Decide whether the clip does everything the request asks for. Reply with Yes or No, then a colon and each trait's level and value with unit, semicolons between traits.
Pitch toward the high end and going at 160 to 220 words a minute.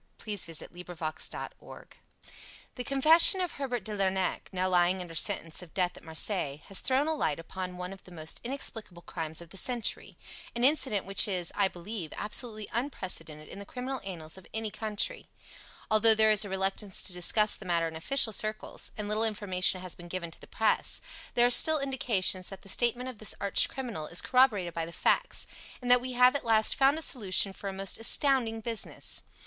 Yes: high, 205 Hz; fast, 205 wpm